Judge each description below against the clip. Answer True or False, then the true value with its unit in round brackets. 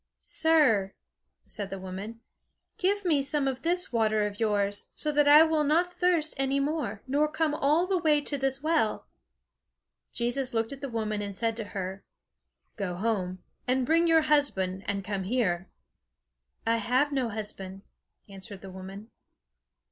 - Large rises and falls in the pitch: True (6.9 semitones)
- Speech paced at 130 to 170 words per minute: True (160 wpm)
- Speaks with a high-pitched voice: True (240 Hz)